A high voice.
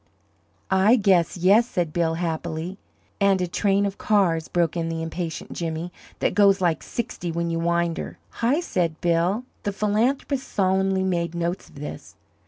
No: medium, 180 Hz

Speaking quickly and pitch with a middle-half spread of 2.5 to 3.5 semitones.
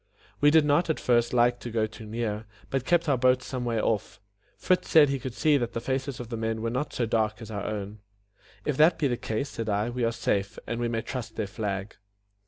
Yes: fast, 245 wpm; average, 3.2 semitones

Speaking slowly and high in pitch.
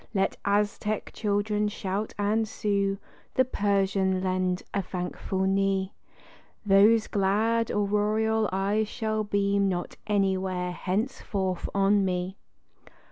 Yes: slow, 105 wpm; high, 200 Hz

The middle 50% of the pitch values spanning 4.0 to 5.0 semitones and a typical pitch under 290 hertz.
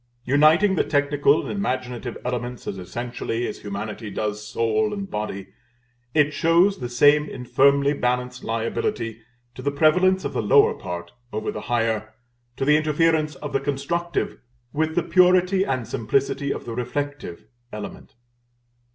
No: wide, 5.4 semitones; medium, 140 Hz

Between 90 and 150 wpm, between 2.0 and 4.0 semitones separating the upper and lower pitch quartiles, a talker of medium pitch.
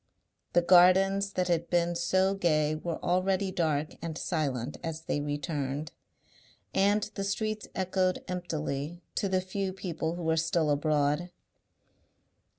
Yes: slow, 135 wpm; average, 3.3 semitones; medium, 175 Hz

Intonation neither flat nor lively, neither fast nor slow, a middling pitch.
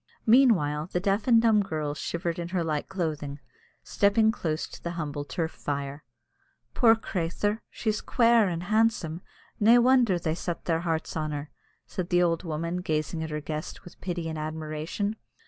Yes: average, 4.9 semitones; average, 170 wpm; medium, 170 Hz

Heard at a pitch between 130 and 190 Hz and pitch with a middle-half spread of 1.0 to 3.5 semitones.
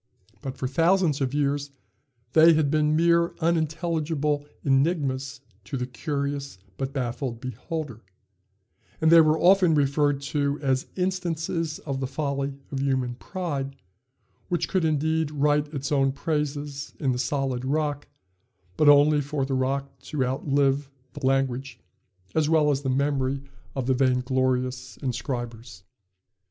Yes: medium, 140 Hz; narrow, 2.5 semitones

